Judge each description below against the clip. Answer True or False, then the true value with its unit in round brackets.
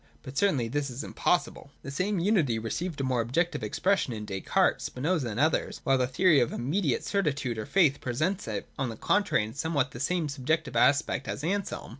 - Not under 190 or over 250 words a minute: True (200 wpm)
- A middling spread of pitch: False (5.7 semitones)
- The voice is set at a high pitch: False (140 Hz)